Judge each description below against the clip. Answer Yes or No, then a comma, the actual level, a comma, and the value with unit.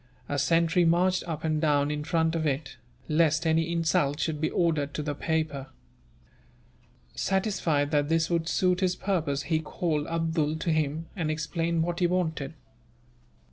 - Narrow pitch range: Yes, narrow, 2.2 semitones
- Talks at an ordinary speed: Yes, average, 160 wpm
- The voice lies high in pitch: No, medium, 160 Hz